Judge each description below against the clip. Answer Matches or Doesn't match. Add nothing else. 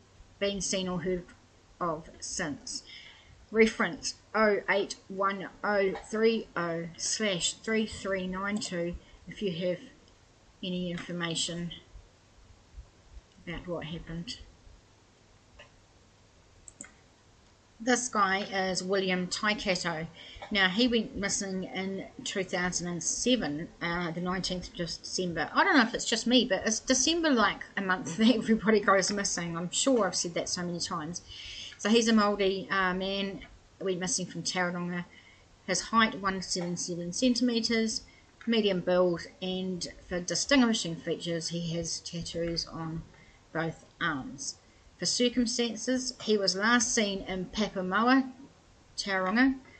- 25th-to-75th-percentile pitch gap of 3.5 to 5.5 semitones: Matches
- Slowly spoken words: Matches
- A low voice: Doesn't match